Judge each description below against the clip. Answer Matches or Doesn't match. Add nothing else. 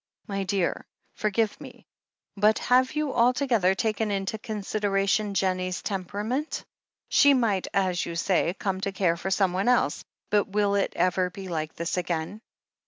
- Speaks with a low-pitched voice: Doesn't match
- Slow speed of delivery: Doesn't match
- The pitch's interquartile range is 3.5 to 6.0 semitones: Doesn't match